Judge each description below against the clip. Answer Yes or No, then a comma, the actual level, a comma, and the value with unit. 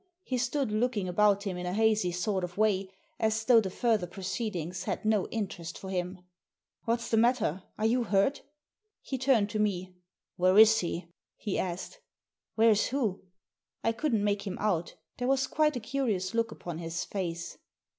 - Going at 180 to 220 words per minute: Yes, average, 190 wpm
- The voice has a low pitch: No, high, 210 Hz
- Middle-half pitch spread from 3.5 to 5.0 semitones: Yes, average, 3.9 semitones